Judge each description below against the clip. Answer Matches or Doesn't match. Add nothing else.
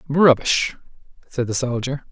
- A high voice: Doesn't match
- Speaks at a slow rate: Matches